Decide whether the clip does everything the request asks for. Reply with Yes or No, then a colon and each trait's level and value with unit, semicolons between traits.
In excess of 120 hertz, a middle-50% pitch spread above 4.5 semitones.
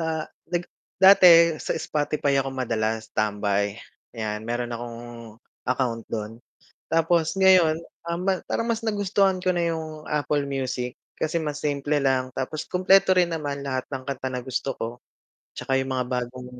Yes: medium, 140 Hz; average, 4.9 semitones